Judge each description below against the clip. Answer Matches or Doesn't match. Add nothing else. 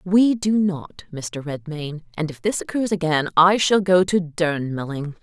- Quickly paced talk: Doesn't match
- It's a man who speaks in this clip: Doesn't match